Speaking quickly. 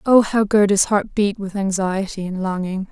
No: average, 185 wpm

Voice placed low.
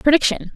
No: very high, 300 Hz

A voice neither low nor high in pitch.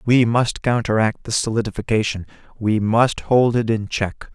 No: low, 115 Hz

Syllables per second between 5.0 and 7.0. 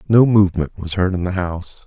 Yes: 6.1 syllables/s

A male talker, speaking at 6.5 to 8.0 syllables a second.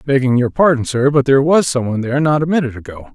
Yes: male; 7.3 syllables/s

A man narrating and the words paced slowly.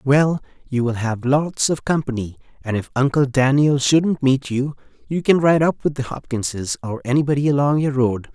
No: male; average, 185 wpm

